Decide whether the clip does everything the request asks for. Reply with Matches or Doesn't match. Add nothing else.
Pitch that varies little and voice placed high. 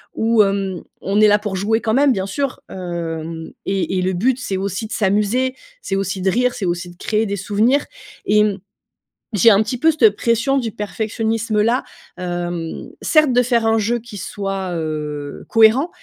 Doesn't match